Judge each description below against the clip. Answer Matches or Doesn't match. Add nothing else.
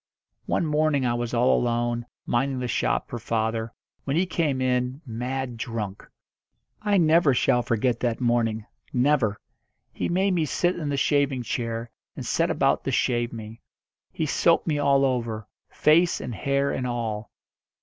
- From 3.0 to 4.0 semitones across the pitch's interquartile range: Matches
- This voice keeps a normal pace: Matches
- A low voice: Matches